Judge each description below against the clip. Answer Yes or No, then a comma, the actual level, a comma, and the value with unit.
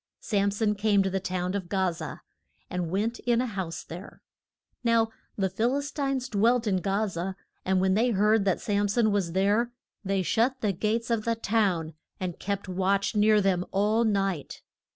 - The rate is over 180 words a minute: Yes, average, 190 wpm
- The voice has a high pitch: Yes, high, 200 Hz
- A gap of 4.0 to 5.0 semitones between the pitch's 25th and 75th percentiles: No, average, 2.9 semitones